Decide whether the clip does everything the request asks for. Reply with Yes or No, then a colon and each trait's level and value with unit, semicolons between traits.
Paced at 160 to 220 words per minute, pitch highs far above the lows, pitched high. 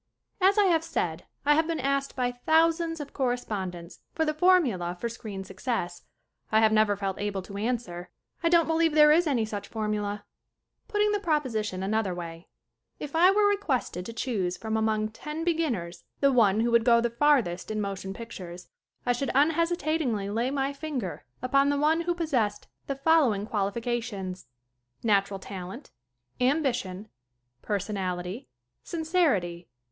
Yes: average, 170 wpm; wide, 7.4 semitones; high, 235 Hz